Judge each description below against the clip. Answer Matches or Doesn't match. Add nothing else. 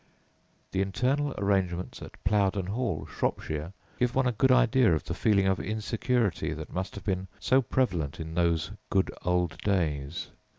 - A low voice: Matches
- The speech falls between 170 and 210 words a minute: Doesn't match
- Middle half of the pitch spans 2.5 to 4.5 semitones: Doesn't match